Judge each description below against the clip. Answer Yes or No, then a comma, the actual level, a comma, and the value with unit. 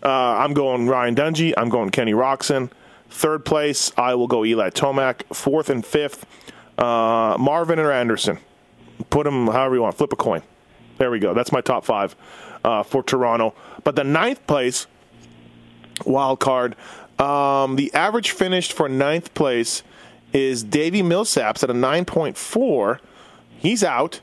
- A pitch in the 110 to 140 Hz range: Yes, low, 135 Hz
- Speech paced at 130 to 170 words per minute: Yes, average, 155 wpm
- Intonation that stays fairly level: No, average, 3.3 semitones